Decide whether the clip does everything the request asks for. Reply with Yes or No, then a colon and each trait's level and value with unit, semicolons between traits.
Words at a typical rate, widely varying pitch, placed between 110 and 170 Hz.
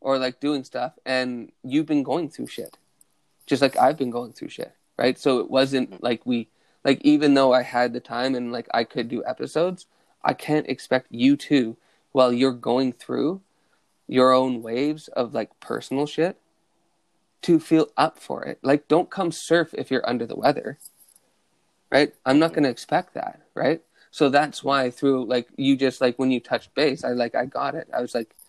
No: average, 195 wpm; average, 2.9 semitones; low, 135 Hz